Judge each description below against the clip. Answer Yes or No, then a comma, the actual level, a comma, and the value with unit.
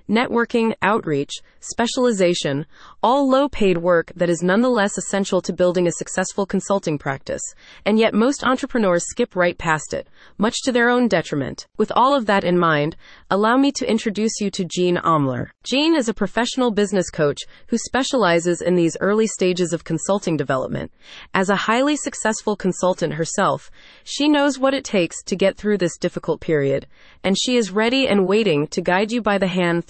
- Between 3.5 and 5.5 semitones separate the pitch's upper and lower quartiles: Yes, average, 5.0 semitones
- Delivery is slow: No, average, 170 wpm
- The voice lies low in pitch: No, high, 195 Hz